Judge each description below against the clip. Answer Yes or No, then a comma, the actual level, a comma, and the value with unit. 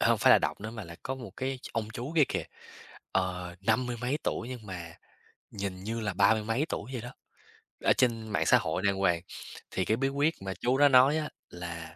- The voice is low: Yes, low, 110 Hz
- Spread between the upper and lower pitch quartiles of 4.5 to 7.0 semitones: Yes, average, 5.1 semitones